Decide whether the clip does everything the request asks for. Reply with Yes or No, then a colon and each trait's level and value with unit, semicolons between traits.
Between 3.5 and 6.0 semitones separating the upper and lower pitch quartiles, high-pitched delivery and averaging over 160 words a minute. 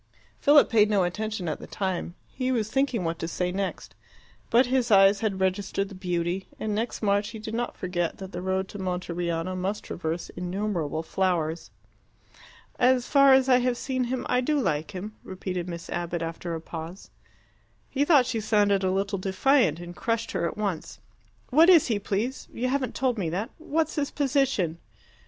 Yes: wide, 5.6 semitones; high, 200 Hz; average, 185 wpm